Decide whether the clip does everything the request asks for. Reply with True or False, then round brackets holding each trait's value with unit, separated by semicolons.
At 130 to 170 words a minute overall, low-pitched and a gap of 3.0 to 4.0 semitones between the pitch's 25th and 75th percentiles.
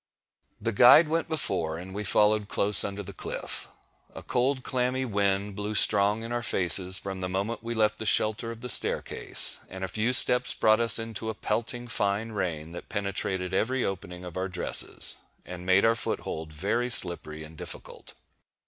False (180 wpm; 105 Hz; 3.6 semitones)